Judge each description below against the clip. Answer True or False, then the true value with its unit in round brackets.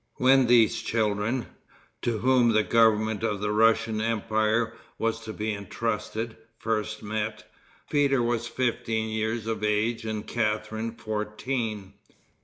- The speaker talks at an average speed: False (125 wpm)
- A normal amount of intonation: False (1.4 semitones)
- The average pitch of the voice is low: True (110 Hz)